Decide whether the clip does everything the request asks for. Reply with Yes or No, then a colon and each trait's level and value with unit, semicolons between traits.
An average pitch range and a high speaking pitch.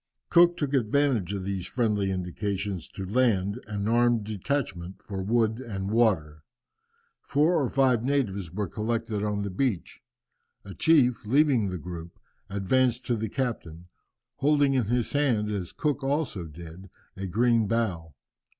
No: average, 5.0 semitones; low, 110 Hz